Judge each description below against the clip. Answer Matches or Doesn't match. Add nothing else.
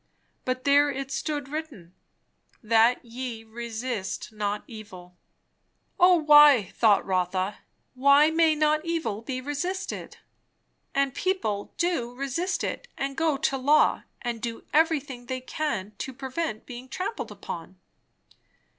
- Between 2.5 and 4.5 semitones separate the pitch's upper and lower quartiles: Doesn't match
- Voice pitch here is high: Matches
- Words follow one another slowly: Matches